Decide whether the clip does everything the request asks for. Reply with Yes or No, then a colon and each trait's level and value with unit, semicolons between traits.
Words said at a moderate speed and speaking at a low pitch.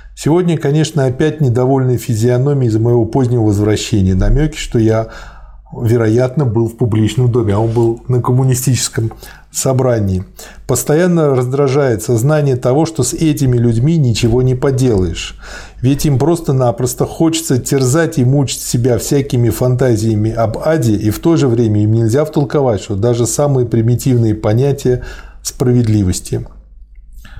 Yes: average, 130 wpm; low, 125 Hz